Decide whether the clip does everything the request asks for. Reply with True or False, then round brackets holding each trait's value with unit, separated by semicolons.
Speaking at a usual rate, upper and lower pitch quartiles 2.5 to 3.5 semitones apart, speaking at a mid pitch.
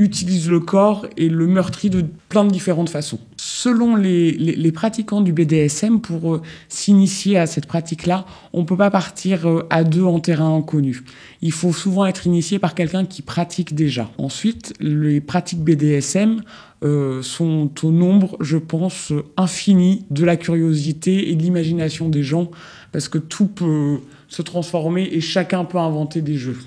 True (175 wpm; 3.1 semitones; 170 Hz)